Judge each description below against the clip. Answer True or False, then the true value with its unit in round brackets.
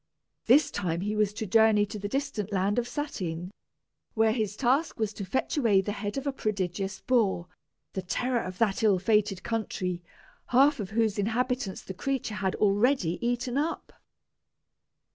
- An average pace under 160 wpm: False (165 wpm)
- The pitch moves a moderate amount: True (4.0 semitones)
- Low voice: False (215 Hz)